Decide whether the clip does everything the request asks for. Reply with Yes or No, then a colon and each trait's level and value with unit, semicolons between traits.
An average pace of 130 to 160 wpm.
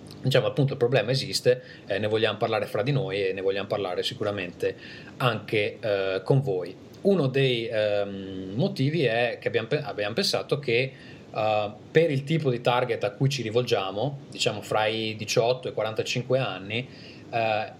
No: fast, 170 wpm